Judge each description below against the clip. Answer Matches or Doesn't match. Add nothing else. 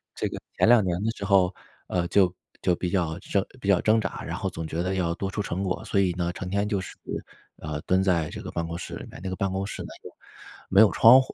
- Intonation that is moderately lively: Doesn't match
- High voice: Doesn't match